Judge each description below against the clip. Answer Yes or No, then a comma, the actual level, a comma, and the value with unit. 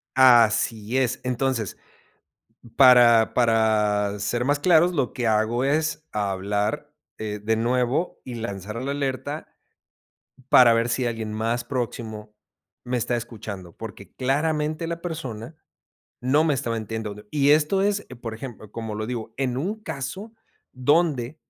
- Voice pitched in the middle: No, low, 120 Hz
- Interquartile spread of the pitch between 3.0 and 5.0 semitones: Yes, average, 4.2 semitones